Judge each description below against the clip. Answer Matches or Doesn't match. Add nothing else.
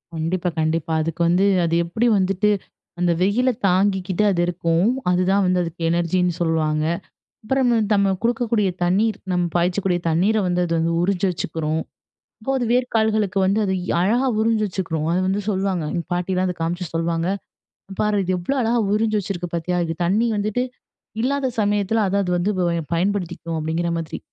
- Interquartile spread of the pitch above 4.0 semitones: Doesn't match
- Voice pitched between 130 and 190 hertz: Matches